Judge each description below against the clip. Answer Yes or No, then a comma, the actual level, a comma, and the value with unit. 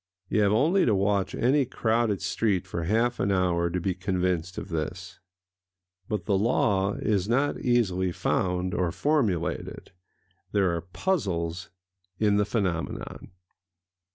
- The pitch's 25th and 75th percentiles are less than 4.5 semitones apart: Yes, average, 3.6 semitones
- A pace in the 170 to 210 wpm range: No, slow, 135 wpm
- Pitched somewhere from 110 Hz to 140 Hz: No, very low, 95 Hz